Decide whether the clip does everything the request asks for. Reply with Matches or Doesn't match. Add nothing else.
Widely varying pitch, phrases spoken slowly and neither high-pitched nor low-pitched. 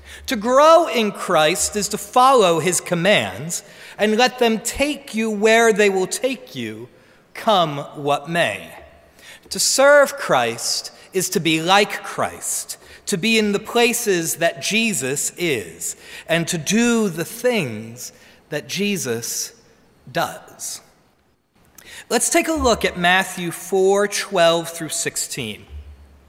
Doesn't match